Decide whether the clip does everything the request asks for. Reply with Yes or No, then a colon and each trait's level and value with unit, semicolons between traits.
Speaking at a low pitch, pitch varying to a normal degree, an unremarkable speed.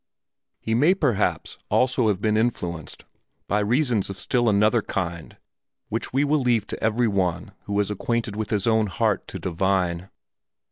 Yes: low, 105 Hz; average, 3.8 semitones; average, 160 wpm